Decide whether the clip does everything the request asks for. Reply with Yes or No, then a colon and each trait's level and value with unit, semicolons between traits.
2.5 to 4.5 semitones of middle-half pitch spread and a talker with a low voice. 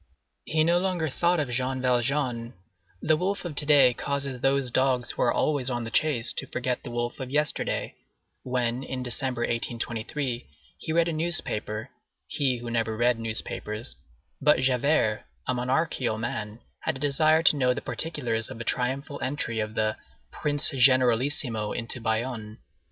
Yes: average, 3.6 semitones; low, 125 Hz